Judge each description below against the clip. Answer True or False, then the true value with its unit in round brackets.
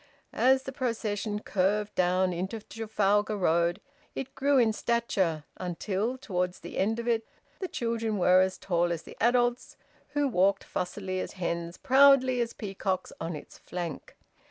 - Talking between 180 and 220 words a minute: False (155 wpm)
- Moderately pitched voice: False (205 Hz)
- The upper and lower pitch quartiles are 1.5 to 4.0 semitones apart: False (4.5 semitones)